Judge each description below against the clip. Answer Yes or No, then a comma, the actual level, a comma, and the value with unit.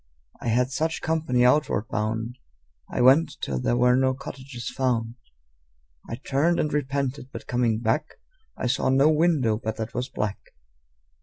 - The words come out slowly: No, average, 155 wpm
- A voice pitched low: Yes, low, 125 Hz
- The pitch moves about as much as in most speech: Yes, average, 3.3 semitones